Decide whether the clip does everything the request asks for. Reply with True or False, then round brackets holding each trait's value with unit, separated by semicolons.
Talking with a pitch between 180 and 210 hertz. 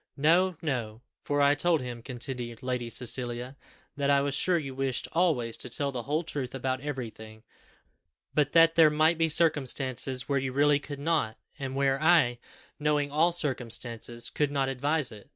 False (140 Hz)